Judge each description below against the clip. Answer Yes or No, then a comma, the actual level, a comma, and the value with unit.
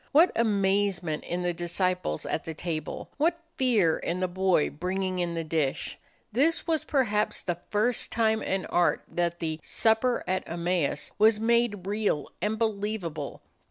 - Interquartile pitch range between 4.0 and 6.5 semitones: Yes, average, 4.3 semitones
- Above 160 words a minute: No, average, 155 wpm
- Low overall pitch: No, high, 190 Hz